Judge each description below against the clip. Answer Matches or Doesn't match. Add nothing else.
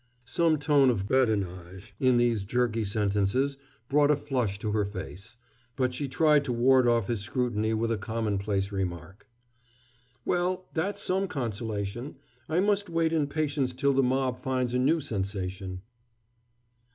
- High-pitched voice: Doesn't match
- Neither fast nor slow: Matches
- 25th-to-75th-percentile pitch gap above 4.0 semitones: Matches